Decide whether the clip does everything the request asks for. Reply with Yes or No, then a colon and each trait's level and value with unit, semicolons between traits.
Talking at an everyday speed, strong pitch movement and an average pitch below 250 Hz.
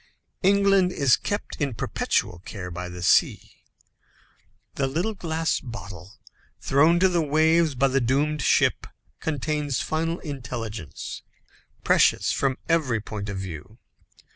No: slow, 125 wpm; wide, 6.9 semitones; medium, 140 Hz